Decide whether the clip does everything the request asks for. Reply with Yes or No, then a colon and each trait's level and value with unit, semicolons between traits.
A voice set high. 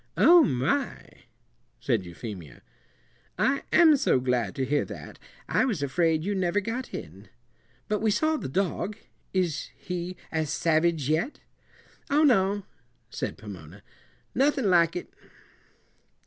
No: medium, 170 Hz